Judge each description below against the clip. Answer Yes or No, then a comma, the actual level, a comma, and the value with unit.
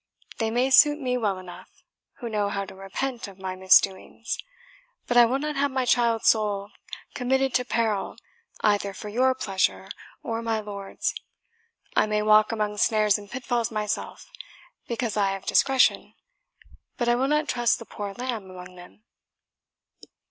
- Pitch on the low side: No, high, 220 Hz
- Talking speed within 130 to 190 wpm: Yes, average, 160 wpm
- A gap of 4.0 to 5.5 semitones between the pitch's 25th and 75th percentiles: No, average, 3.6 semitones